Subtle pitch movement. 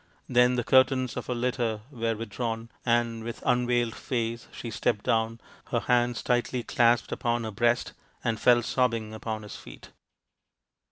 Yes: narrow, 1.4 semitones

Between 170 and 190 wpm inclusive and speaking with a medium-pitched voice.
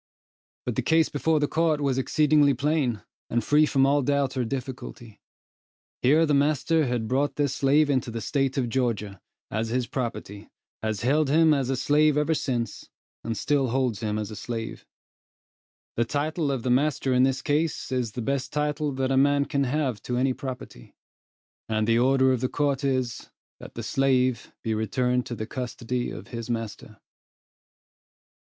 No: average, 175 wpm; low, 130 Hz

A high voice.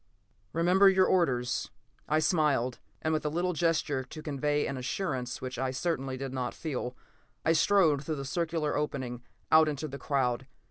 No: medium, 150 Hz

